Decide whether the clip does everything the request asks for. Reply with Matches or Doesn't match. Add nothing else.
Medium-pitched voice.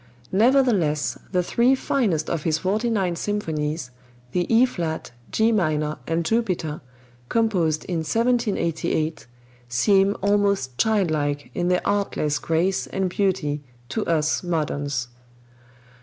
Matches